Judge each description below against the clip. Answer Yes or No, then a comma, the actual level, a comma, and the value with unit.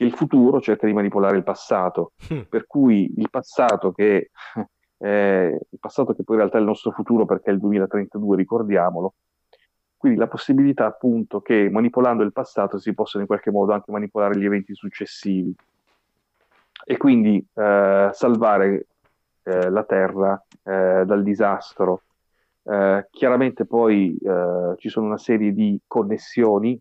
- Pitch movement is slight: Yes, narrow, 2.2 semitones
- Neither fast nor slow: Yes, average, 150 wpm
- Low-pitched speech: Yes, low, 100 Hz